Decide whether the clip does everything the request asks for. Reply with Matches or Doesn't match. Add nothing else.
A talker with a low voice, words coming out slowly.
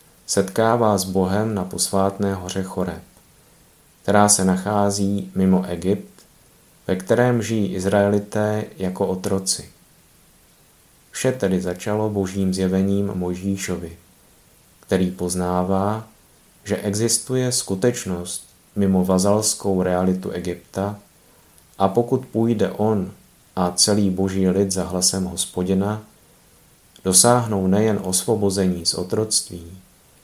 Matches